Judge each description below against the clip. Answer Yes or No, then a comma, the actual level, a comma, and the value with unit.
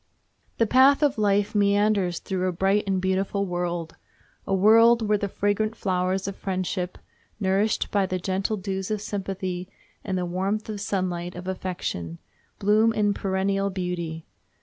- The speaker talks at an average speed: Yes, average, 145 wpm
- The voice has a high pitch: Yes, high, 195 Hz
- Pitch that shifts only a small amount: Yes, narrow, 2.1 semitones